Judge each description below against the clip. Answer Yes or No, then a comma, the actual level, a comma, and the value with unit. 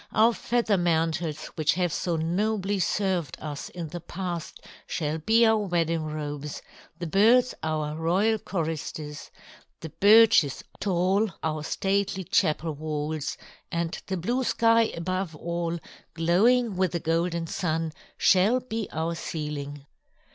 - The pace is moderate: No, slow, 130 wpm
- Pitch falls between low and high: Yes, medium, 170 Hz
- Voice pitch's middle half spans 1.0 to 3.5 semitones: No, average, 4.1 semitones